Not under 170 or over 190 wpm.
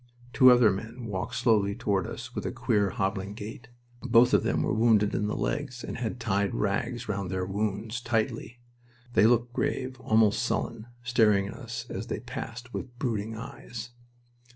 Yes: average, 175 wpm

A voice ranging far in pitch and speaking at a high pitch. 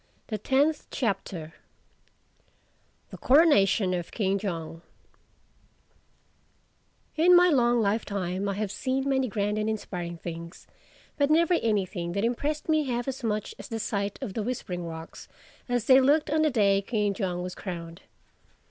Yes: wide, 6.0 semitones; high, 215 Hz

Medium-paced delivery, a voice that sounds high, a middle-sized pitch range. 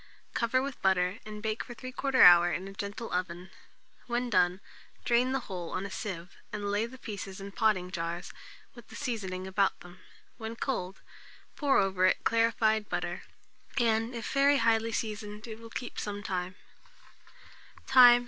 Yes: average, 160 wpm; high, 210 Hz; average, 3.9 semitones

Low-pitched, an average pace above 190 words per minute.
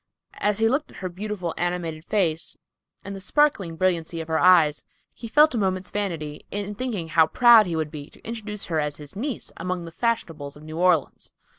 No: medium, 180 Hz; average, 200 wpm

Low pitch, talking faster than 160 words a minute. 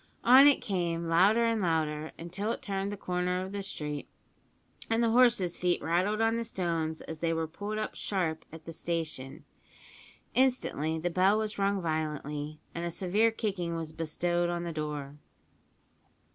No: medium, 175 Hz; average, 170 wpm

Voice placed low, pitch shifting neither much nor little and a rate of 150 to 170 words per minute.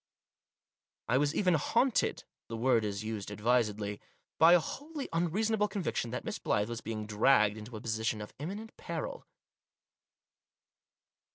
No: low, 120 Hz; wide, 8.5 semitones; average, 155 wpm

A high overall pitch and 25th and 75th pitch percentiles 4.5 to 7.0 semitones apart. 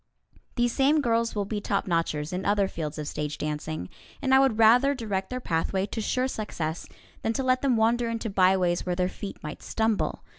Yes: high, 210 Hz; average, 5.3 semitones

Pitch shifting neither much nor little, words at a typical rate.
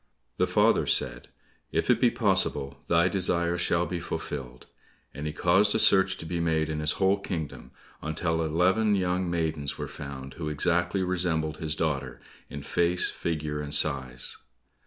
Yes: average, 3.1 semitones; average, 160 wpm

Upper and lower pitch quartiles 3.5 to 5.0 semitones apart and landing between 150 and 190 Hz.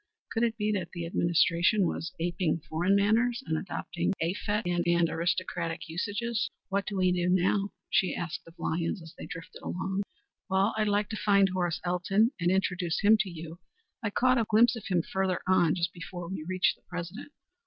No: average, 3.1 semitones; medium, 185 Hz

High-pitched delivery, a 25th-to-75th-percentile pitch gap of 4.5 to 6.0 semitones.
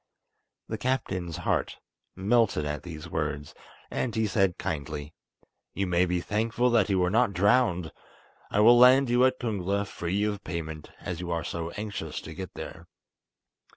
No: very low, 95 Hz; average, 4.9 semitones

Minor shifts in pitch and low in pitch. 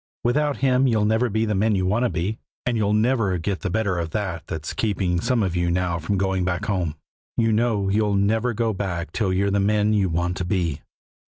No: average, 3.6 semitones; low, 100 Hz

